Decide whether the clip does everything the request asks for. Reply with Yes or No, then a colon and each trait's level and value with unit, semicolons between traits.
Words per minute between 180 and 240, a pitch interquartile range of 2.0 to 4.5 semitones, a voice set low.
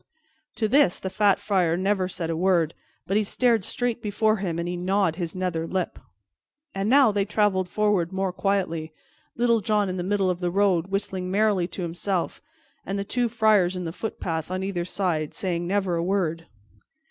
No: average, 190 wpm; average, 2.8 semitones; high, 190 Hz